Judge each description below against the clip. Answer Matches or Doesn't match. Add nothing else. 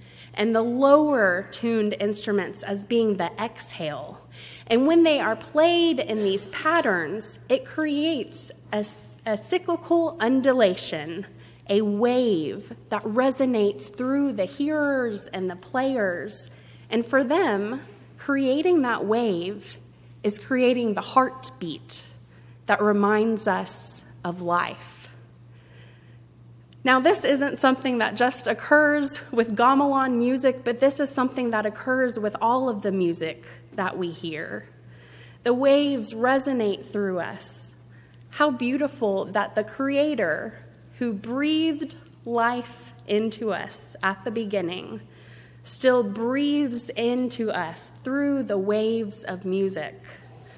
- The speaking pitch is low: Doesn't match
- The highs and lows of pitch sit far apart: Matches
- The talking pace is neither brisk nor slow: Doesn't match